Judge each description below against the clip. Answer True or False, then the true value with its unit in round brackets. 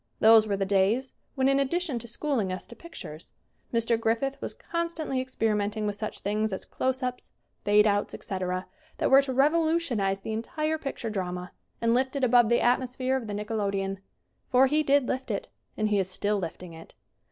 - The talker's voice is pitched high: True (230 Hz)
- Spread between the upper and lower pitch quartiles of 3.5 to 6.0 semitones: True (4.7 semitones)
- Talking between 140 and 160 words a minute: False (195 wpm)